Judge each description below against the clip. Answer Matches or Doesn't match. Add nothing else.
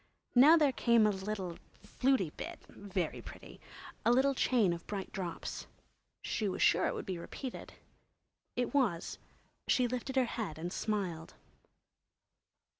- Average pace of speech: Doesn't match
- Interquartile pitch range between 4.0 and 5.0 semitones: Doesn't match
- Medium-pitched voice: Doesn't match